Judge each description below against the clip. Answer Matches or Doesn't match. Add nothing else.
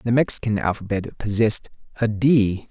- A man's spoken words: Matches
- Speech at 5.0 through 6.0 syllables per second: Matches